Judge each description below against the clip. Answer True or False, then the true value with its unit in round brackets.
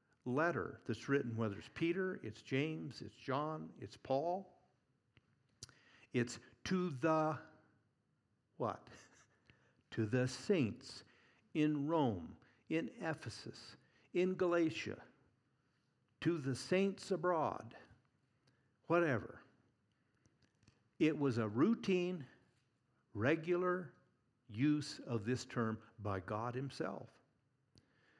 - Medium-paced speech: False (90 wpm)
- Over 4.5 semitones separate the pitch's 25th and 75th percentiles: True (5.2 semitones)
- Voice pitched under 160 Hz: True (135 Hz)